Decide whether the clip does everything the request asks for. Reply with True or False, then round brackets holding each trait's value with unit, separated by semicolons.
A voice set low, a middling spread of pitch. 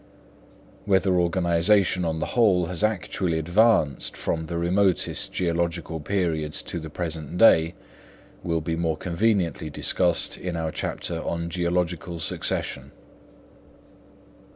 False (85 Hz; 2.0 semitones)